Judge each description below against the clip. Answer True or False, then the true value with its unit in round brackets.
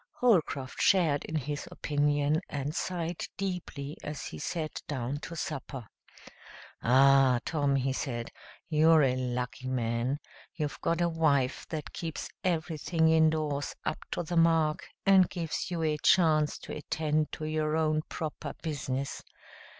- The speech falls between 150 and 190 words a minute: False (140 wpm)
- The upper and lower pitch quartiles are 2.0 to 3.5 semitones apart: True (2.8 semitones)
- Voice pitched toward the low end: False (155 Hz)